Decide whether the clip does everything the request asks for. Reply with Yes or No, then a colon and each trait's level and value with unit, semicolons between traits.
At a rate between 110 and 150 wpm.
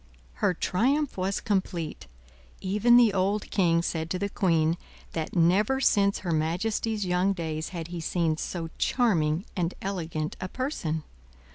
Yes: average, 145 wpm